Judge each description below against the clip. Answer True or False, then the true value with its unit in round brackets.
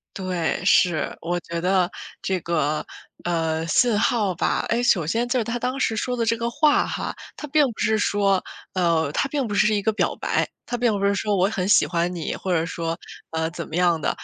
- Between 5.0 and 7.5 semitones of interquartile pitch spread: True (5.3 semitones)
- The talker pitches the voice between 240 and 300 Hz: False (190 Hz)